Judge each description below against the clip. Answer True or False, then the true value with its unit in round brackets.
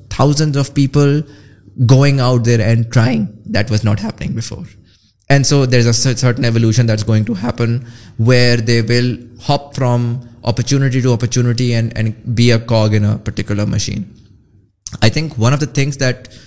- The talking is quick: False (175 wpm)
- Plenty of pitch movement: False (2.9 semitones)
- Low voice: True (120 Hz)